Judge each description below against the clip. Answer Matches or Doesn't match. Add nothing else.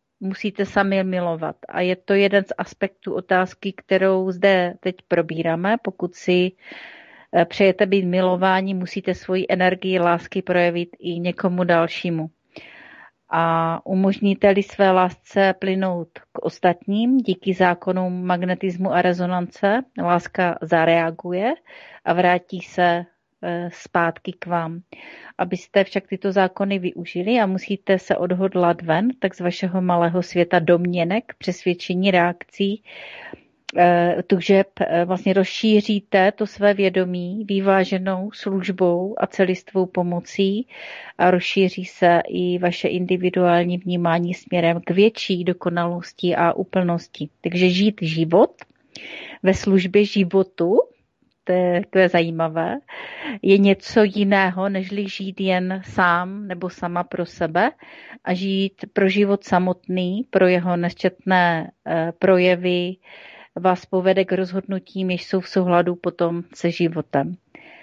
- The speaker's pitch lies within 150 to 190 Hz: Matches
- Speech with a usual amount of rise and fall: Doesn't match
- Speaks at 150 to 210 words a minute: Doesn't match